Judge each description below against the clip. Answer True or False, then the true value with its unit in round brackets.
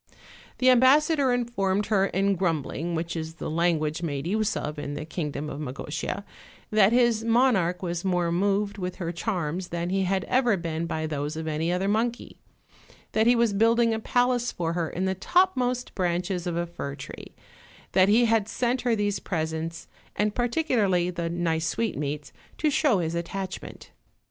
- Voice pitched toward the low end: False (185 Hz)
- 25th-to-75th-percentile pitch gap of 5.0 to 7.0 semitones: True (5.3 semitones)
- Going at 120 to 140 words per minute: False (175 wpm)